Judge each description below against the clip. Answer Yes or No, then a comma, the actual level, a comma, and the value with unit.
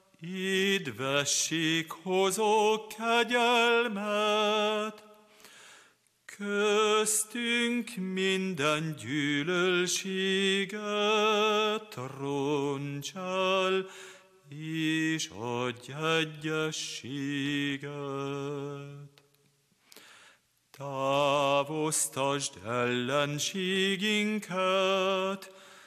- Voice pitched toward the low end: No, medium, 180 Hz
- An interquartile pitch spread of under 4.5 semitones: No, wide, 6.5 semitones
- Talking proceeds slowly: Yes, slow, 30 wpm